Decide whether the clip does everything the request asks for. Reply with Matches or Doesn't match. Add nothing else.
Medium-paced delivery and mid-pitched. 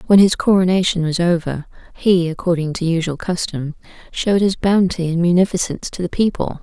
Matches